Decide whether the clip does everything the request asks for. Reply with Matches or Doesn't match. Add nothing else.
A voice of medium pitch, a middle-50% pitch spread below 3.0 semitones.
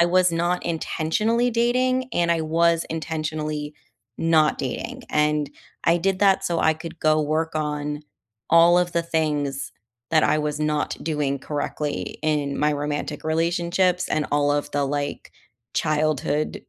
Matches